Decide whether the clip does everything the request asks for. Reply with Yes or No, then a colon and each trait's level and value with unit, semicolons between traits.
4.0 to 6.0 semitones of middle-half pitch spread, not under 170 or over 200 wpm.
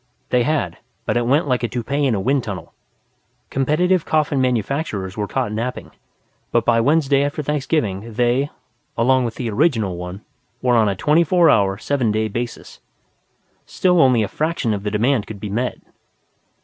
Yes: average, 5.0 semitones; average, 175 wpm